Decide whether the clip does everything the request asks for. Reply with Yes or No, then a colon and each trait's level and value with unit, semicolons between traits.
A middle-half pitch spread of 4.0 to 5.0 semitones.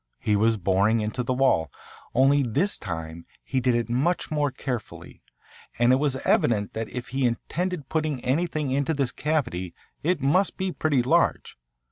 Yes: average, 4.7 semitones